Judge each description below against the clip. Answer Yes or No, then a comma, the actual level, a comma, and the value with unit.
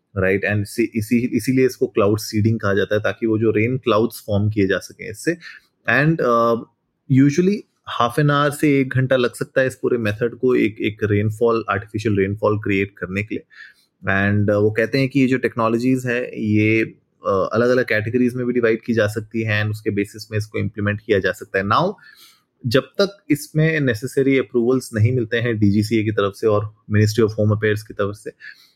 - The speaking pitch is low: Yes, low, 115 Hz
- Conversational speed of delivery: No, fast, 195 wpm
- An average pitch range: Yes, average, 3.4 semitones